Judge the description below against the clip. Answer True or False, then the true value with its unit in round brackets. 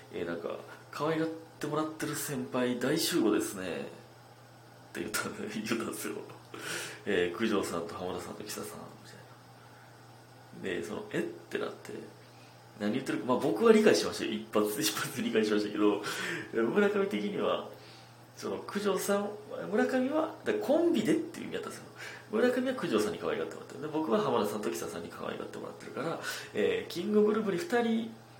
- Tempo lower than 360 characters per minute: False (365 characters per minute)